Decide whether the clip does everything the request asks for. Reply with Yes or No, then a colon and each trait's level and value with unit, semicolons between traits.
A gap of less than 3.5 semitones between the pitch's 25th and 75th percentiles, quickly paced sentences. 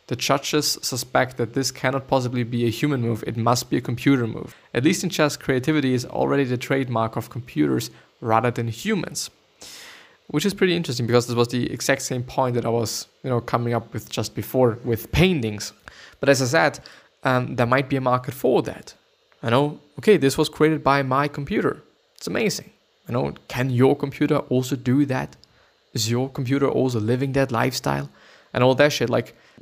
No: average, 3.1 semitones; average, 195 wpm